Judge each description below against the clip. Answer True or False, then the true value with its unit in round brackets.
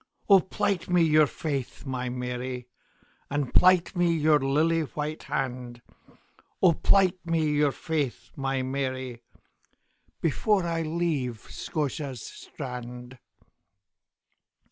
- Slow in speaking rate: True (95 wpm)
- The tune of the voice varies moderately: True (4.5 semitones)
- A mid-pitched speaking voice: True (145 Hz)